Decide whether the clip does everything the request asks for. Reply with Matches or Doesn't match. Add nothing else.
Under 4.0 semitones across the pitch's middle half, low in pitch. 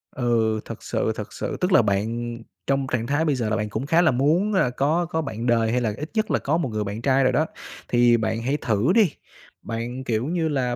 Doesn't match